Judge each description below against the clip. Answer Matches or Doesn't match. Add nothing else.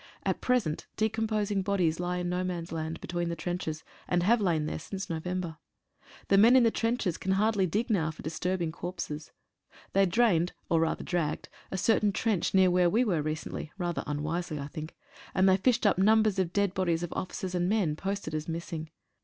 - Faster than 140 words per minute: Matches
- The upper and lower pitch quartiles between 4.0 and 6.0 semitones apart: Doesn't match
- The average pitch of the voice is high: Doesn't match